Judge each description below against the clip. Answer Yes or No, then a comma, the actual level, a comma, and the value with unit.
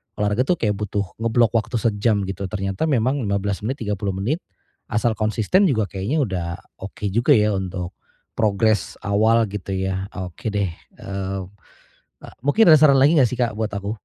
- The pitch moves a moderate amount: Yes, average, 3.4 semitones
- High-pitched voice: No, low, 105 Hz